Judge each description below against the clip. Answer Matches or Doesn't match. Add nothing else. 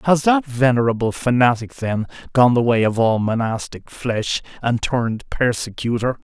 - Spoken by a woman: Doesn't match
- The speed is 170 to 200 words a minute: Doesn't match